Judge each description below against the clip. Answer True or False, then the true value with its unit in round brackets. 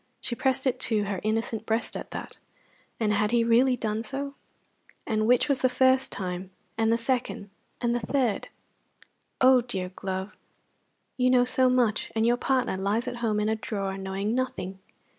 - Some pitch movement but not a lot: True (3.3 semitones)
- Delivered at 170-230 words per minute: True (180 wpm)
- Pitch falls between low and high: False (230 Hz)